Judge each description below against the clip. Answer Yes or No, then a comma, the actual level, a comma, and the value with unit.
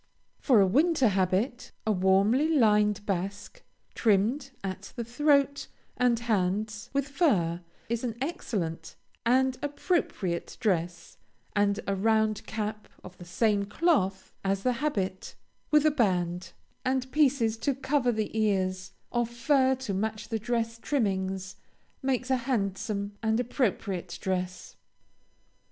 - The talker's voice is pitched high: Yes, high, 220 Hz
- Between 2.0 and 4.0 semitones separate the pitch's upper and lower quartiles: No, average, 5.1 semitones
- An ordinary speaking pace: No, slow, 130 wpm